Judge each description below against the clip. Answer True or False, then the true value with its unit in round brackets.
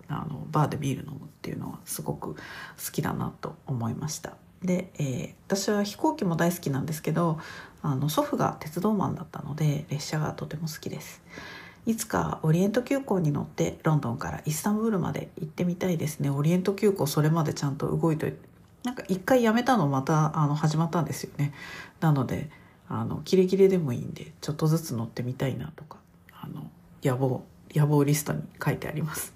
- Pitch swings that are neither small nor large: True (4.3 semitones)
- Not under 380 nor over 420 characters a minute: True (400 characters per minute)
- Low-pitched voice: False (160 Hz)